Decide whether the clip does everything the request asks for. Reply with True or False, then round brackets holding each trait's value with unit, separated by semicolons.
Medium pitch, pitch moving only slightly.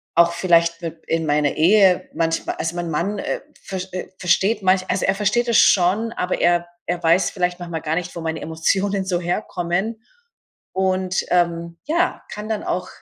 True (180 Hz; 2.3 semitones)